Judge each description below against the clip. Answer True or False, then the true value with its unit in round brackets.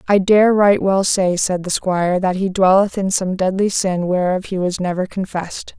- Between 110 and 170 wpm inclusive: False (205 wpm)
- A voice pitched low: False (190 Hz)